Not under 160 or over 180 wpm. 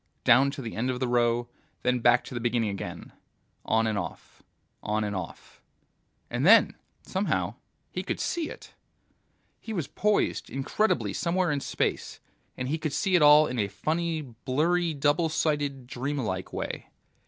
Yes: average, 165 wpm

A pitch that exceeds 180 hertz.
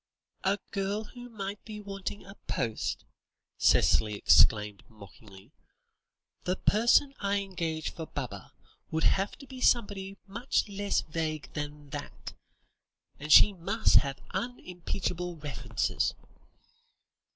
Yes: high, 190 Hz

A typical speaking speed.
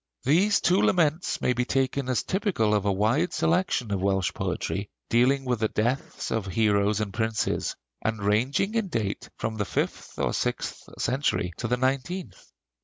Yes: average, 170 wpm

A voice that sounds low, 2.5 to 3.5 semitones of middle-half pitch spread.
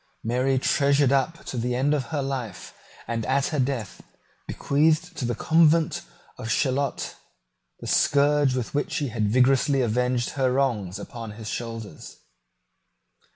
Yes: low, 130 Hz; average, 3.2 semitones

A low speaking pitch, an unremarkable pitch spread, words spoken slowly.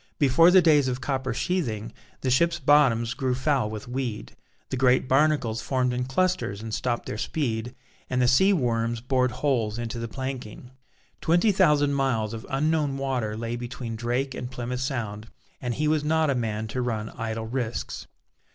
No: low, 125 Hz; average, 3.6 semitones; average, 175 wpm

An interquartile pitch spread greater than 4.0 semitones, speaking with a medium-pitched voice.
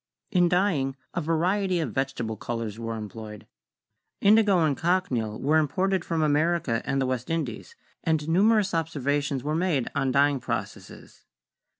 Yes: average, 5.2 semitones; medium, 150 Hz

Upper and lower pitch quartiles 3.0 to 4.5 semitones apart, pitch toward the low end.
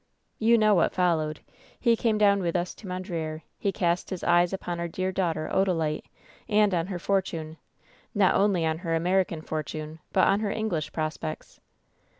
No: average, 3.4 semitones; medium, 175 Hz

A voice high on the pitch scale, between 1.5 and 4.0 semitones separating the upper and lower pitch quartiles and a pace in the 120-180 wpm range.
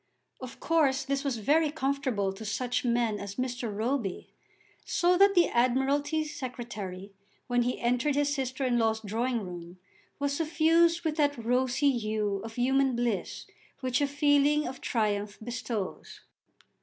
No: very high, 255 Hz; average, 4.4 semitones; average, 145 wpm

